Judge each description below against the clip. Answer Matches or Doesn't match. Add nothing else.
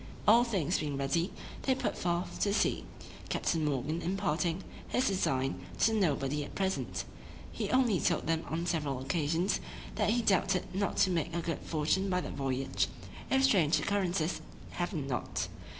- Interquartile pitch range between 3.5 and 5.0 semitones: Matches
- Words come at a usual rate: Matches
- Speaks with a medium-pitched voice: Matches